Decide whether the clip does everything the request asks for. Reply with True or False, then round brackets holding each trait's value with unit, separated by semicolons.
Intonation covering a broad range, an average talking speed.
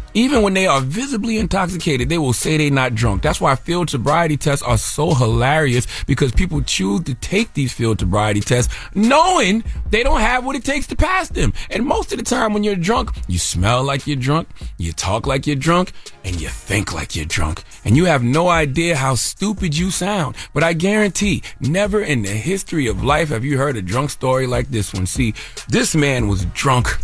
False (8.3 semitones; 210 wpm)